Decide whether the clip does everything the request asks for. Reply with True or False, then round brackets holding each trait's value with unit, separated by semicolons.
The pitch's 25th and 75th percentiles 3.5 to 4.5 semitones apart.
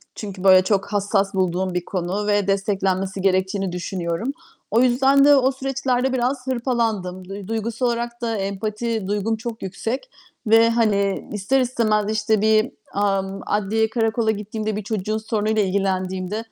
False (3.1 semitones)